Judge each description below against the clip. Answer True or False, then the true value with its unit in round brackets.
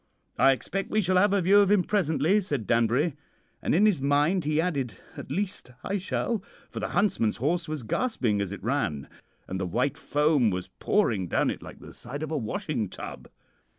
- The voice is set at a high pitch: False (150 Hz)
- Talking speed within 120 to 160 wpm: False (195 wpm)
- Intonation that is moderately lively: False (8.2 semitones)